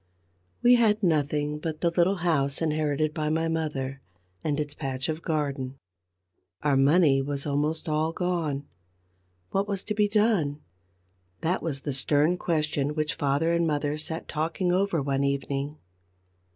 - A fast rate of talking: No, average, 150 wpm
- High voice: No, medium, 155 Hz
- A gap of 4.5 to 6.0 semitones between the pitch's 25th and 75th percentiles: No, average, 2.9 semitones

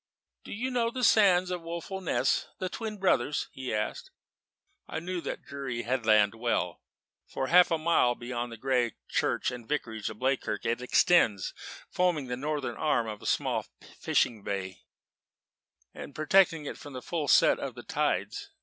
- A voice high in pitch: No, low, 135 Hz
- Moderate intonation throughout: No, wide, 6.8 semitones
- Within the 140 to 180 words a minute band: Yes, average, 165 wpm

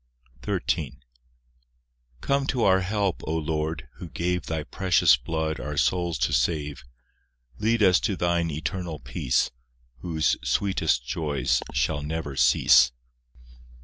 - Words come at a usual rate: No, slow, 120 wpm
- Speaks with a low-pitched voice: Yes, very low, 80 Hz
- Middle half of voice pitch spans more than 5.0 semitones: No, average, 3.8 semitones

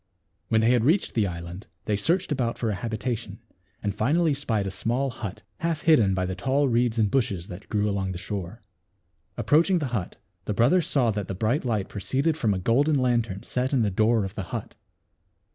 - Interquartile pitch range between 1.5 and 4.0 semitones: No, average, 5.1 semitones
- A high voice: No, low, 115 Hz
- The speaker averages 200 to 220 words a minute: Yes, fast, 205 wpm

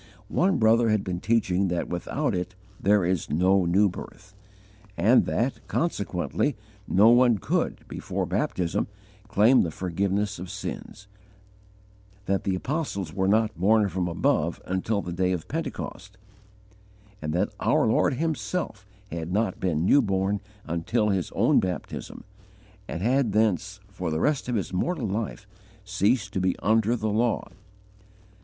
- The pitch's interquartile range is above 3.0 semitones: Yes, average, 3.5 semitones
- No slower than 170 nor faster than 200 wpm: No, average, 145 wpm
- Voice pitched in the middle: No, low, 100 Hz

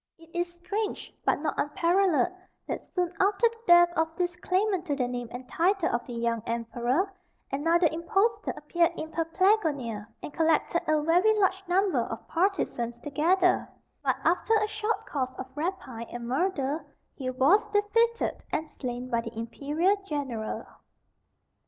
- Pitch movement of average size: No, wide, 6.6 semitones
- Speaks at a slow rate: No, average, 150 wpm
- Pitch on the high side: Yes, very high, 330 Hz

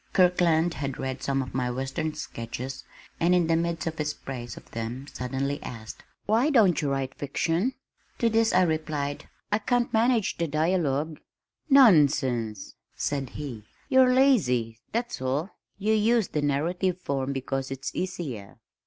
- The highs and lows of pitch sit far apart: Yes, wide, 5.7 semitones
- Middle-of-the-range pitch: Yes, medium, 150 Hz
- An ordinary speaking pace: Yes, average, 155 wpm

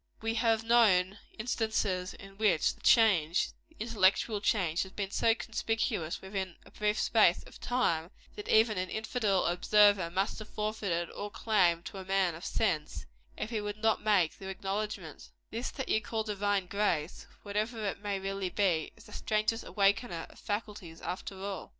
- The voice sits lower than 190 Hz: No, high, 205 Hz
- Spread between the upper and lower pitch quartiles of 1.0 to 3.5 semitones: Yes, average, 2.9 semitones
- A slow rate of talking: No, average, 170 wpm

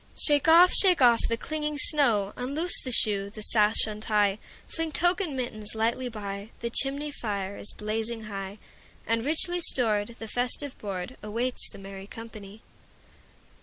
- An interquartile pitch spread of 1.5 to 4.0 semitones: No, average, 5.1 semitones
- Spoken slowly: Yes, slow, 130 wpm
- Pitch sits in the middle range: No, high, 230 Hz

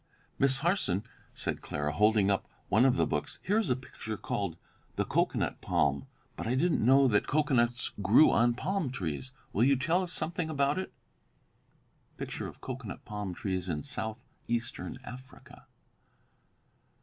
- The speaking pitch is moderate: No, low, 125 Hz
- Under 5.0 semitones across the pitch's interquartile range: No, wide, 5.5 semitones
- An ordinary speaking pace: Yes, average, 150 wpm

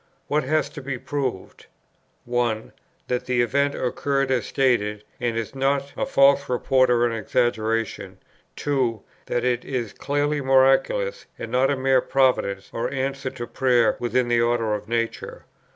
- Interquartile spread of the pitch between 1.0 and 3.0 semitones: Yes, narrow, 2.6 semitones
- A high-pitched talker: No, low, 125 Hz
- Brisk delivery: No, average, 155 wpm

